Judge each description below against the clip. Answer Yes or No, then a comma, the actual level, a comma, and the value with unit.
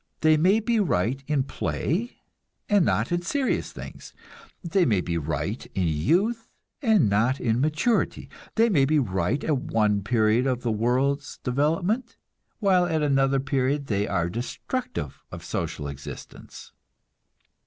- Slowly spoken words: No, average, 145 wpm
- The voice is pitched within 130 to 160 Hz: Yes, low, 135 Hz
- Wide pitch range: Yes, wide, 8.2 semitones